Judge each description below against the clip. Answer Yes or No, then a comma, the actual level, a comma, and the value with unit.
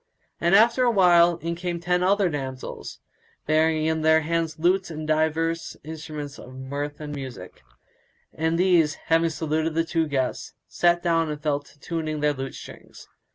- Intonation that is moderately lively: No, narrow, 2.2 semitones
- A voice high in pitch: No, medium, 160 Hz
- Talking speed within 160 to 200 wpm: Yes, average, 165 wpm